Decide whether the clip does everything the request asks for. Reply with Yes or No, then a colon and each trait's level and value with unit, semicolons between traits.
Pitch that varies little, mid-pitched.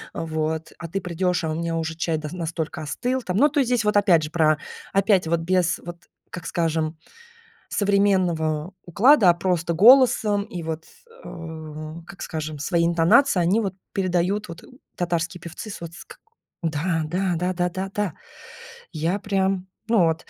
No: average, 3.2 semitones; medium, 175 Hz